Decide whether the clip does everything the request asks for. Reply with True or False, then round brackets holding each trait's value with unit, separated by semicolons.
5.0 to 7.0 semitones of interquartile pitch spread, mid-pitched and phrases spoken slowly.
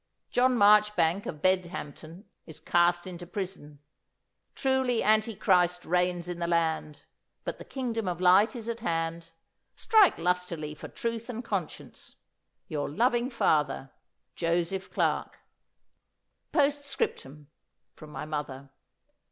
True (5.5 semitones; 180 Hz; 115 wpm)